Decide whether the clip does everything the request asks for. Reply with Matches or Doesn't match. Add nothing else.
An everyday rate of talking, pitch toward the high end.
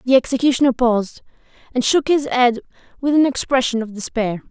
Matches